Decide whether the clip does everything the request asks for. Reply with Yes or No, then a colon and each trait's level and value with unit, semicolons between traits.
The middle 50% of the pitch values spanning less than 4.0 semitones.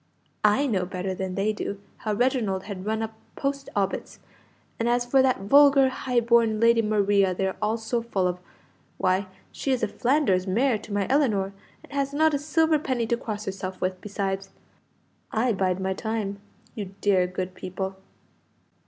No: average, 4.3 semitones